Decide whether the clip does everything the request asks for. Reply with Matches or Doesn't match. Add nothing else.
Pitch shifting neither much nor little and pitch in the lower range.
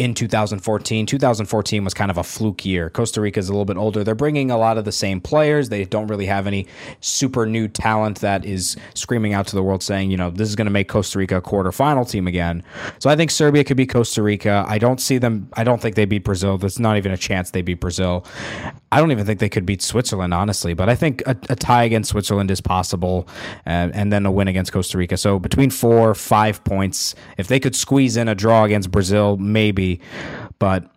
Matches